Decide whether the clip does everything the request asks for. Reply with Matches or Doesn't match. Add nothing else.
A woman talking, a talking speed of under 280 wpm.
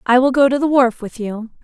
Doesn't match